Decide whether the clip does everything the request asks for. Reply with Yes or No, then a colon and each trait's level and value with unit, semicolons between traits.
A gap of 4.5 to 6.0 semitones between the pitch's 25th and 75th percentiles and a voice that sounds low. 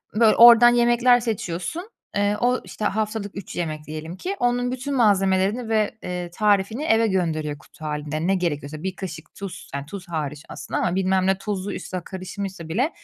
No: average, 4.8 semitones; high, 195 Hz